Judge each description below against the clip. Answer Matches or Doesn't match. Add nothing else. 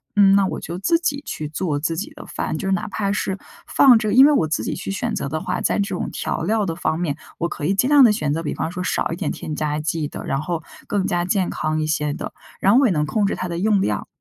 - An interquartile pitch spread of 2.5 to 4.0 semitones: Doesn't match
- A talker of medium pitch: Matches